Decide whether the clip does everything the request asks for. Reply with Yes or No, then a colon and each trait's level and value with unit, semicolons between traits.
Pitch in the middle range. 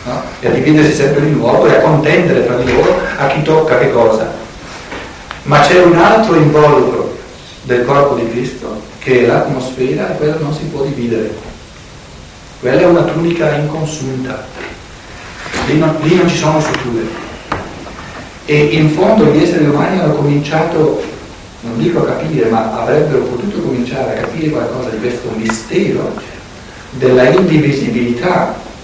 Yes: medium, 150 Hz